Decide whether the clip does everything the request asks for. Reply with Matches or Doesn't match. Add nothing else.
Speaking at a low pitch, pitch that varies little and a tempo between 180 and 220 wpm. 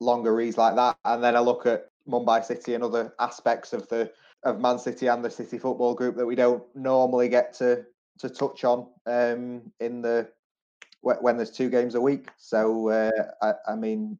Matches